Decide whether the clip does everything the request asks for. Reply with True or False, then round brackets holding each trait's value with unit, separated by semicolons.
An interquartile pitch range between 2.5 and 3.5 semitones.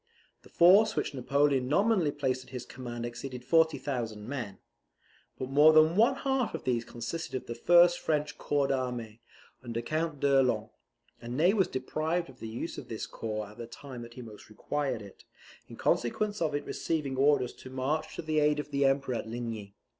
False (4.5 semitones)